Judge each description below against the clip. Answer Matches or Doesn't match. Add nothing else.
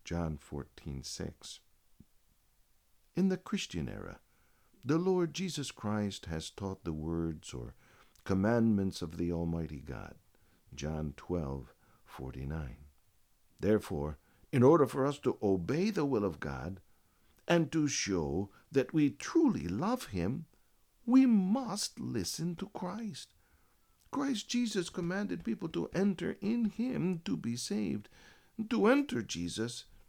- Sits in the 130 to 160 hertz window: Doesn't match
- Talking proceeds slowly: Matches